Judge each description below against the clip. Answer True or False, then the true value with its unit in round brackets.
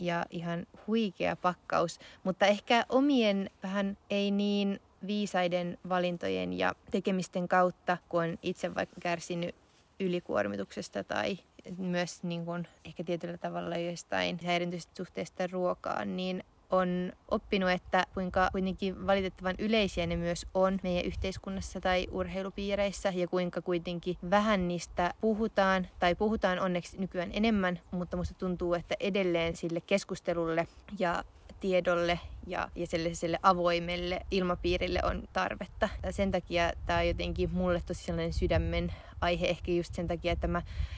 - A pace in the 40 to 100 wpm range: False (130 wpm)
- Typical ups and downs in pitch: False (1.8 semitones)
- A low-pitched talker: False (180 Hz)